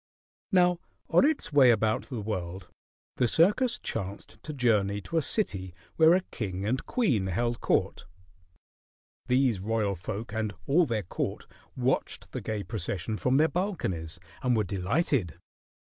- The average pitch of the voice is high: No, low, 115 Hz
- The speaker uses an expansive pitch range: Yes, wide, 7.5 semitones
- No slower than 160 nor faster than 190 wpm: No, average, 145 wpm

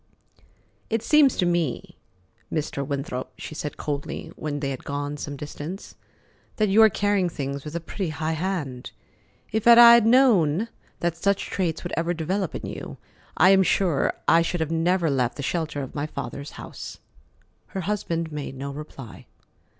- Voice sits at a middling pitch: Yes, medium, 165 Hz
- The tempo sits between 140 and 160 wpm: No, average, 170 wpm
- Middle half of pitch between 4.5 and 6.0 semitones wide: Yes, average, 4.9 semitones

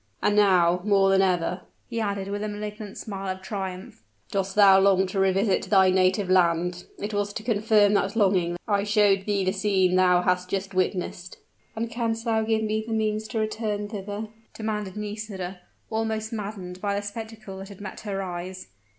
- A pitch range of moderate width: No, narrow, 2.2 semitones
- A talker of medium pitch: No, high, 200 Hz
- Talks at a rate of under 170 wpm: No, average, 185 wpm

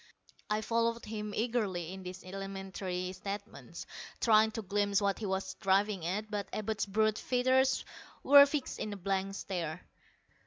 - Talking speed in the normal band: Yes, average, 150 wpm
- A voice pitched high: Yes, high, 200 Hz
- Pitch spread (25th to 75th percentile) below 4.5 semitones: Yes, narrow, 2.4 semitones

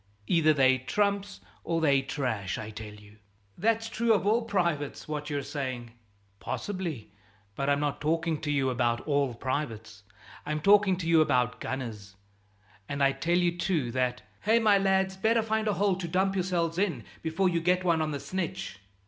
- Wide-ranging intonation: Yes, wide, 6.4 semitones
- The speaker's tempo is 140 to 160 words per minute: No, average, 185 wpm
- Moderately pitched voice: Yes, medium, 160 Hz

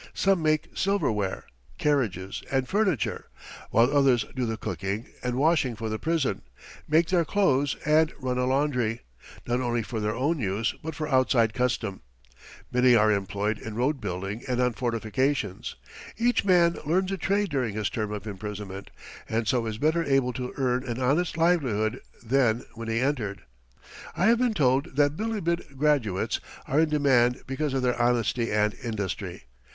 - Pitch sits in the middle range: No, low, 125 Hz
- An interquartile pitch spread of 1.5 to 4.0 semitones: No, average, 5.3 semitones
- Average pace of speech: Yes, average, 165 wpm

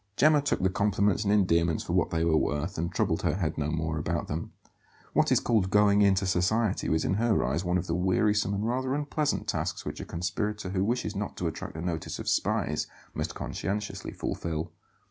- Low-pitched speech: Yes, very low, 95 Hz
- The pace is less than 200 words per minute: No, fast, 205 wpm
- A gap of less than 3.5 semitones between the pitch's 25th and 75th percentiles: No, average, 4.0 semitones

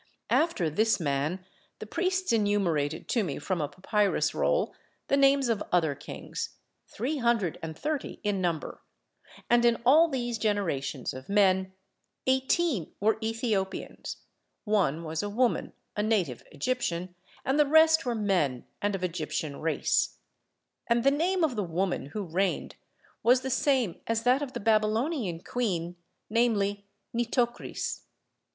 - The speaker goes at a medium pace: Yes, average, 145 wpm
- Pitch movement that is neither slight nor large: No, wide, 5.8 semitones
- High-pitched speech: Yes, high, 210 Hz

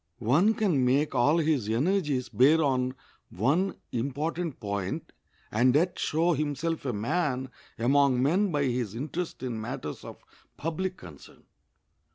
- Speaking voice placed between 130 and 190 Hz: Yes, medium, 140 Hz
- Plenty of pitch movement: No, average, 4.9 semitones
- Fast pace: No, slow, 135 wpm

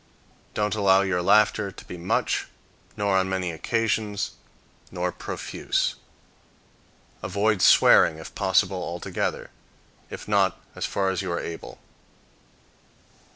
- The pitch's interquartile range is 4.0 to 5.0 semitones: No, narrow, 2.4 semitones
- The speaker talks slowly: Yes, slow, 110 wpm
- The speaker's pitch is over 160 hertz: No, very low, 95 Hz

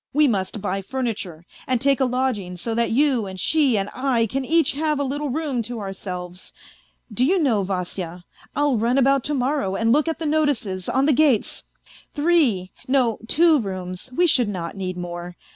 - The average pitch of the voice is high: Yes, high, 240 Hz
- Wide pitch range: Yes, wide, 6.8 semitones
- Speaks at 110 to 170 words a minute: No, average, 190 wpm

